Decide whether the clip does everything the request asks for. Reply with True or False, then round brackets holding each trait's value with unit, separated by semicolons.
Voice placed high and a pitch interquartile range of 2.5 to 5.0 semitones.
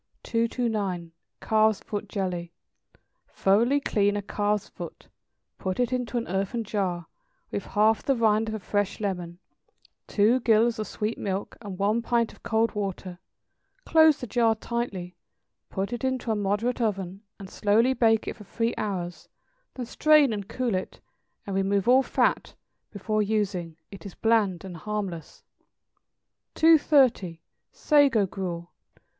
True (210 Hz; 3.3 semitones)